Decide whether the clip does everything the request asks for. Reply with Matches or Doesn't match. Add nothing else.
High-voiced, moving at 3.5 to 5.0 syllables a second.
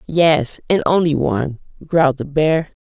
Doesn't match